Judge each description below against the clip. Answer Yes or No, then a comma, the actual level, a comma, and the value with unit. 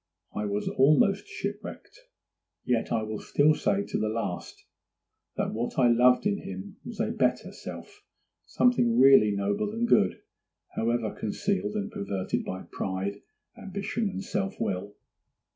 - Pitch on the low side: Yes, low, 120 Hz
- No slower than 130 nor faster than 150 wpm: Yes, average, 140 wpm